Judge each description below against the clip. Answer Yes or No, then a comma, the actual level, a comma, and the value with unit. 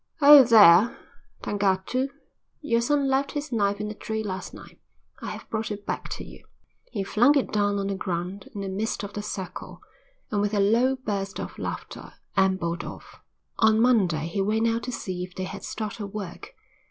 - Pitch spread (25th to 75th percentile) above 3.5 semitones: No, average, 3.2 semitones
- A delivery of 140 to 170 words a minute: No, average, 190 wpm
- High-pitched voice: Yes, high, 205 Hz